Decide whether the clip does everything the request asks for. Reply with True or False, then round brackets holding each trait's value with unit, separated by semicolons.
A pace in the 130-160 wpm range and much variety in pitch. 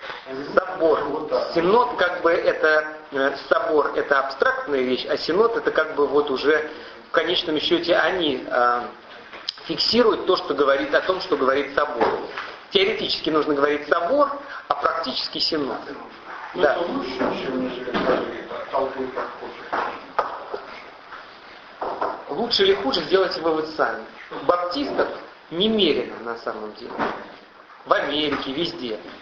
False (115 wpm; 6.9 semitones)